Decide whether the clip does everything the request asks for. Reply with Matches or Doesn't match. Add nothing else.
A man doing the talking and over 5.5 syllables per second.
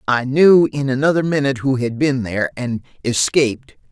Doesn't match